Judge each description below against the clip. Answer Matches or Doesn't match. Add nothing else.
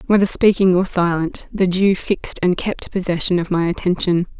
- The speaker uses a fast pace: Doesn't match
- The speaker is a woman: Matches